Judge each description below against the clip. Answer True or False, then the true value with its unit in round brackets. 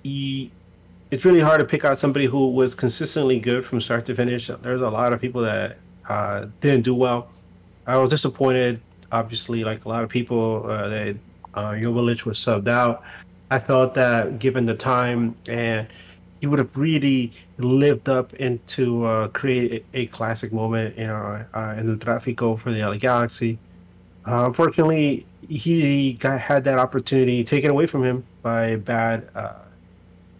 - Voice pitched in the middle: False (120 Hz)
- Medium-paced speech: True (175 wpm)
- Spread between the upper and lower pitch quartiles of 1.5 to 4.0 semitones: True (3.0 semitones)